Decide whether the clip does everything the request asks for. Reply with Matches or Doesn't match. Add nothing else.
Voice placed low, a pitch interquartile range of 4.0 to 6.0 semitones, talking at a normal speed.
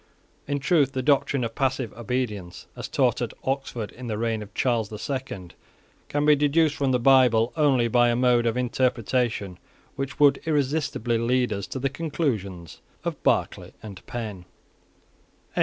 Doesn't match